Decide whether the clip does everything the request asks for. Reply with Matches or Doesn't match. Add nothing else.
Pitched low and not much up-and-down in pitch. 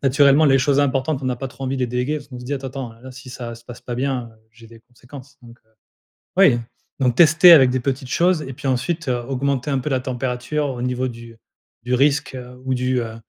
Matches